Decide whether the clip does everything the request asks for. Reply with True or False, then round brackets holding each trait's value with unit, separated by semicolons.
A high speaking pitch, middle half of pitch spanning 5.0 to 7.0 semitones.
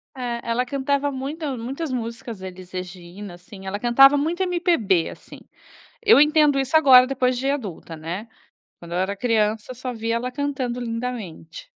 True (245 Hz; 5.4 semitones)